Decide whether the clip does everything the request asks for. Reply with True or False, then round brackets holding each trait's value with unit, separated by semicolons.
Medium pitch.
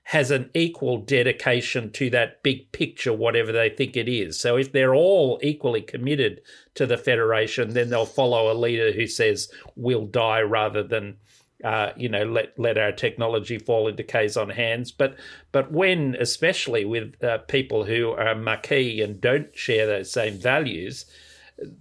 False (125 Hz)